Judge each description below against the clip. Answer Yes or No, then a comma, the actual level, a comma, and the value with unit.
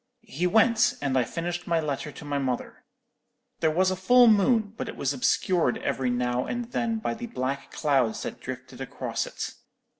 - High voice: No, medium, 160 Hz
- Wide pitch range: Yes, wide, 8.5 semitones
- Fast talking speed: No, average, 185 wpm